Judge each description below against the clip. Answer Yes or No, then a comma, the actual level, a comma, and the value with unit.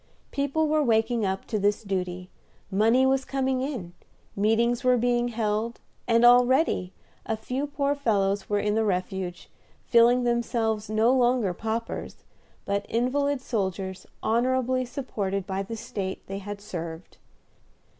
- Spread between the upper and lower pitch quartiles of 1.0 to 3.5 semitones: No, average, 4.0 semitones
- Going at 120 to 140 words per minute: Yes, slow, 135 wpm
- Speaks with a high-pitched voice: Yes, high, 225 Hz